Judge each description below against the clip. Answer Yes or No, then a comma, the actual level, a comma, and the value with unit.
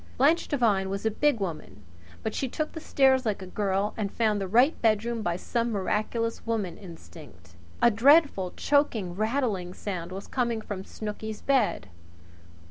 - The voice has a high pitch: Yes, high, 215 Hz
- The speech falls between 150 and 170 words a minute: Yes, average, 160 wpm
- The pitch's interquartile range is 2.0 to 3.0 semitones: No, average, 4.1 semitones